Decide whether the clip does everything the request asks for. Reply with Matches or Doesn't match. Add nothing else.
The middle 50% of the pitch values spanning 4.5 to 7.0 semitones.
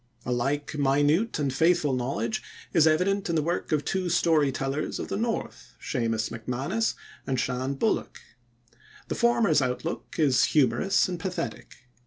Matches